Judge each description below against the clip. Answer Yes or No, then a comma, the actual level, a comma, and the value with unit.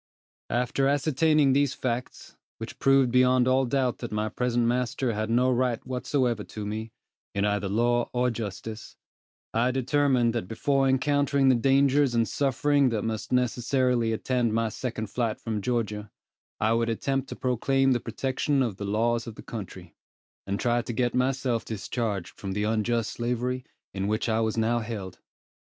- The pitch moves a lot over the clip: No, narrow, 2.6 semitones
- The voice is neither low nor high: No, low, 120 Hz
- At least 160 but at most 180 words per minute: Yes, average, 165 wpm